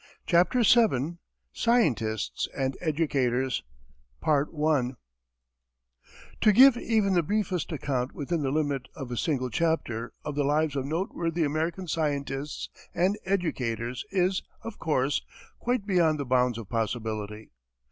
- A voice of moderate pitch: Yes, medium, 145 Hz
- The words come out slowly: Yes, slow, 120 wpm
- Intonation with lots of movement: Yes, wide, 5.8 semitones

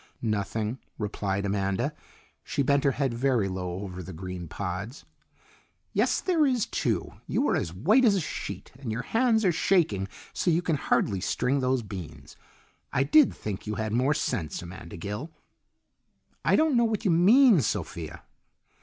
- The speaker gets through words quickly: No, average, 165 wpm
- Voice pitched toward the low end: Yes, low, 120 Hz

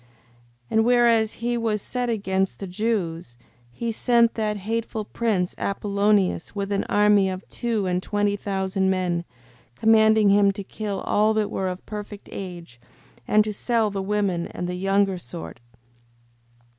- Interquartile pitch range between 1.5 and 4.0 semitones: Yes, narrow, 2.4 semitones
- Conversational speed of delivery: Yes, average, 155 wpm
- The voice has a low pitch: No, high, 205 Hz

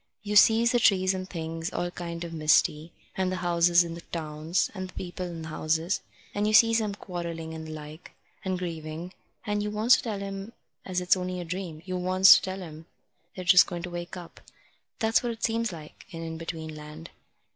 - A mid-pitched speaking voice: Yes, medium, 180 Hz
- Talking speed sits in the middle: No, fast, 215 wpm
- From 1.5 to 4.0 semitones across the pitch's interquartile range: Yes, average, 3.0 semitones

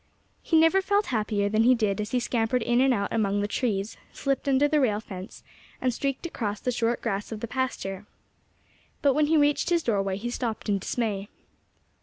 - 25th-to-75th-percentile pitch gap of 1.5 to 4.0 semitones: No, average, 4.6 semitones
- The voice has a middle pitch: No, high, 230 Hz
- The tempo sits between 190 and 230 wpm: Yes, average, 200 wpm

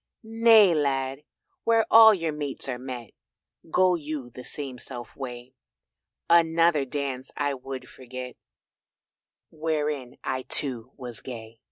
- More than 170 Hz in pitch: No, low, 135 Hz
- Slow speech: Yes, slow, 120 wpm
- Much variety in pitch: No, average, 3.8 semitones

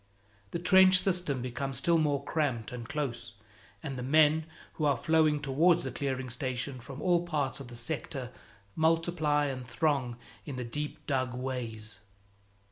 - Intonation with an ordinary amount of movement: Yes, average, 3.9 semitones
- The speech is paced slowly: No, average, 155 wpm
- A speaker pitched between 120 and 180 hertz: Yes, medium, 140 Hz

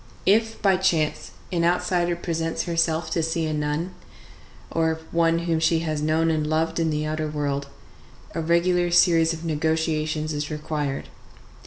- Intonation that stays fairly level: Yes, narrow, 1.6 semitones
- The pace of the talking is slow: No, average, 155 wpm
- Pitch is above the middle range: No, medium, 160 Hz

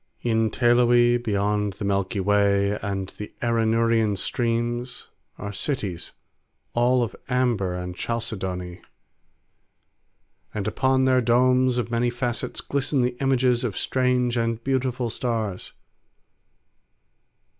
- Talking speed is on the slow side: Yes, slow, 110 wpm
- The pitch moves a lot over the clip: No, average, 3.3 semitones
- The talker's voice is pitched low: Yes, low, 115 Hz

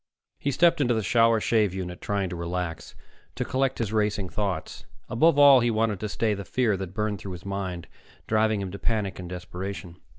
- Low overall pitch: Yes, low, 105 Hz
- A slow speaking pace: No, average, 200 wpm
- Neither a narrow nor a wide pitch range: Yes, average, 3.7 semitones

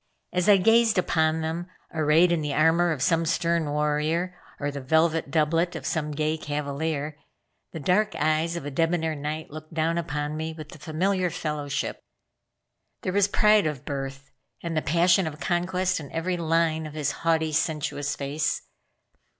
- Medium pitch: Yes, medium, 160 Hz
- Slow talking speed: No, average, 165 wpm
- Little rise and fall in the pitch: Yes, narrow, 2.2 semitones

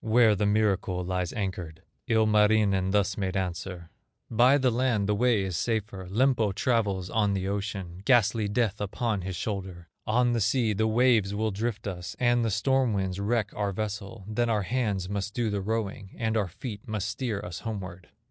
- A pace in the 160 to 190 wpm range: Yes, average, 180 wpm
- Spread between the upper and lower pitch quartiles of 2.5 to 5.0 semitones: Yes, average, 2.9 semitones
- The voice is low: Yes, low, 105 Hz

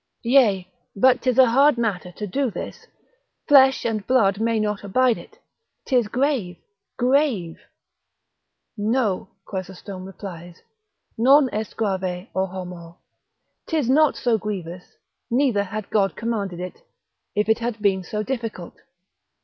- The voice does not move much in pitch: No, average, 4.9 semitones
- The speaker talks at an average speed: No, slow, 130 wpm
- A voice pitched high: Yes, high, 215 Hz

